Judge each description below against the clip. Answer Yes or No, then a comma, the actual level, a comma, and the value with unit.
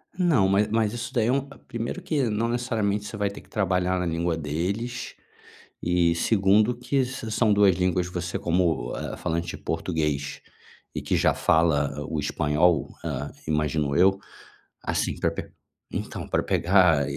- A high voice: No, very low, 95 Hz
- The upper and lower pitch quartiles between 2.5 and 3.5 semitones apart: No, average, 5.3 semitones